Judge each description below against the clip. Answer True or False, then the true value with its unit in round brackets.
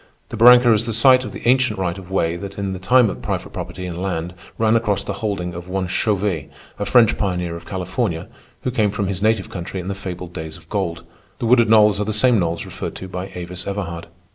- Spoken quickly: True (235 wpm)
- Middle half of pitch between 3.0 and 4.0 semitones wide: True (3.5 semitones)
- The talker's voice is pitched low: True (95 Hz)